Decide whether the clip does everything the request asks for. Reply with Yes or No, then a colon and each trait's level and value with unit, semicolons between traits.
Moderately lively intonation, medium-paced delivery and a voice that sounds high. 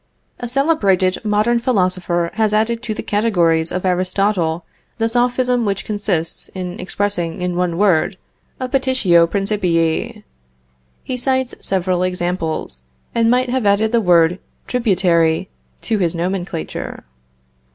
No: average, 4.5 semitones; slow, 125 wpm; high, 195 Hz